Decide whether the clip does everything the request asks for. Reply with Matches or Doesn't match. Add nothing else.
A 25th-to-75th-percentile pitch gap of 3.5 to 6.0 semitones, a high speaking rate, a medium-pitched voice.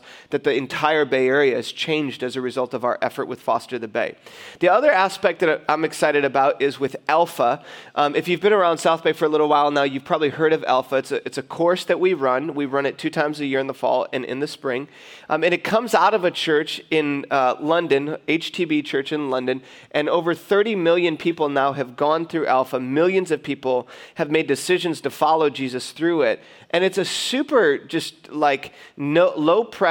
Matches